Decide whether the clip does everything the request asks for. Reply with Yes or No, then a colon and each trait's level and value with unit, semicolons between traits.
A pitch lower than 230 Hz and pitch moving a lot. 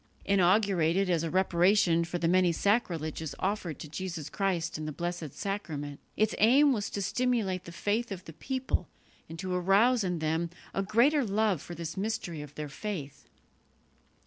No: medium, 185 Hz; average, 3.8 semitones